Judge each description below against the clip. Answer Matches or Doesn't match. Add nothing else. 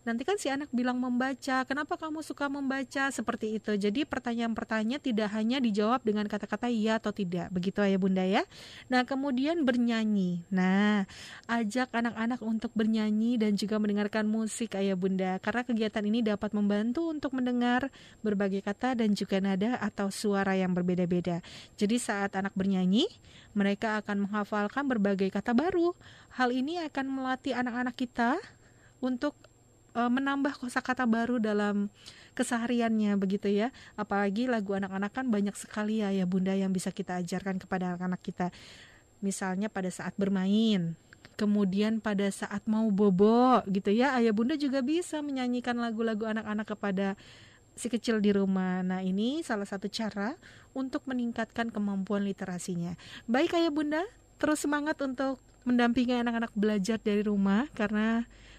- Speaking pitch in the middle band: Doesn't match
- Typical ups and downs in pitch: Matches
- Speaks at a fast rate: Matches